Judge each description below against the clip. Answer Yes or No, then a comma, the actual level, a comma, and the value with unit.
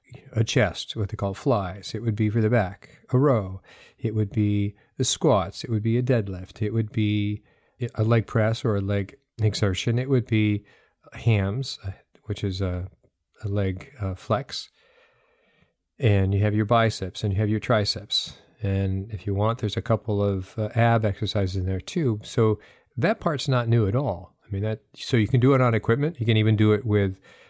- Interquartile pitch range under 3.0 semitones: Yes, narrow, 2.5 semitones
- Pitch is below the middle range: Yes, low, 110 Hz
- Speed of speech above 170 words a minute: Yes, average, 200 wpm